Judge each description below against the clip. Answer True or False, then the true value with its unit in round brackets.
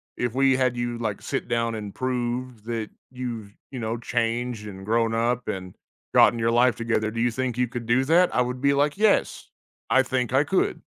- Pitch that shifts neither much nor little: False (2.0 semitones)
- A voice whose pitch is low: True (120 Hz)